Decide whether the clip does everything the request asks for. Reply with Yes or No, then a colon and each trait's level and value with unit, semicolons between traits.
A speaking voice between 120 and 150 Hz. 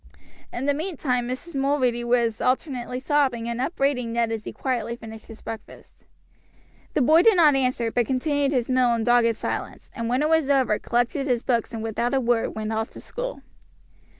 No: very high, 250 Hz